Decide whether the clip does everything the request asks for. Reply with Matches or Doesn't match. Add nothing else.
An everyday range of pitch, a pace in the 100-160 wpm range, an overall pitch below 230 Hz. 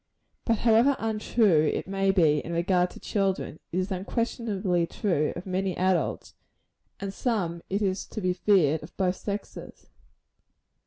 Matches